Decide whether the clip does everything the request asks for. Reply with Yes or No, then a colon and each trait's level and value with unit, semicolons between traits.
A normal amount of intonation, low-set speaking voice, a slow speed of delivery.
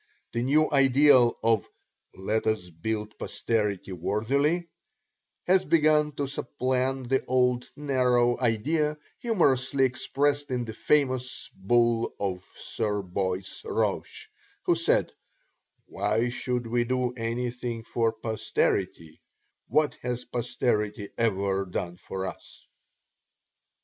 Yes: average, 3.9 semitones; low, 120 Hz; slow, 110 wpm